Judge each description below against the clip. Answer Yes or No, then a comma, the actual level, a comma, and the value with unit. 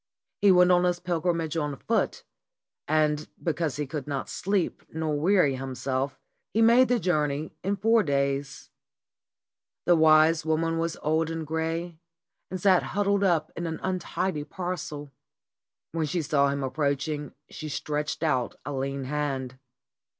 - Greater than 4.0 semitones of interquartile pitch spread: No, average, 3.5 semitones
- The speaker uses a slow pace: No, average, 150 wpm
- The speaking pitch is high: No, medium, 155 Hz